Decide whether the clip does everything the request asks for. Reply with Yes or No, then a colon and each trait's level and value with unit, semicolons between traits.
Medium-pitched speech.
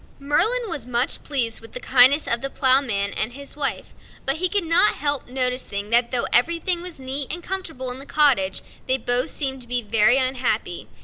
No: very high, 260 Hz